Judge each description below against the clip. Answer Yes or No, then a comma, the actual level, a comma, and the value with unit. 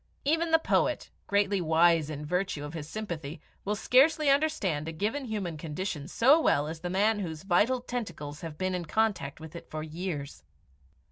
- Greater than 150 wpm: Yes, average, 180 wpm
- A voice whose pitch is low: No, medium, 180 Hz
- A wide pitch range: Yes, wide, 5.9 semitones